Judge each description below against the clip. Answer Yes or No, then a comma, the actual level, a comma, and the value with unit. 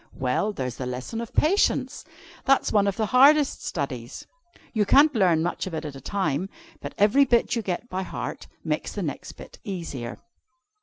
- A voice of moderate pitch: No, high, 195 Hz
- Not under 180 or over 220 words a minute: Yes, average, 185 wpm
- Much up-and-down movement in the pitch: Yes, wide, 8.5 semitones